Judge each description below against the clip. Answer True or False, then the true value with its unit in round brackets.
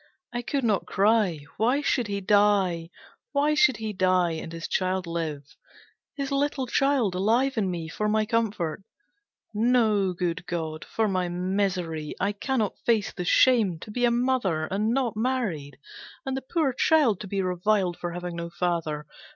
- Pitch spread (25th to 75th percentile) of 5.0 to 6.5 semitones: True (5.3 semitones)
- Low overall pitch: False (200 Hz)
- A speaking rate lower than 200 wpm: True (165 wpm)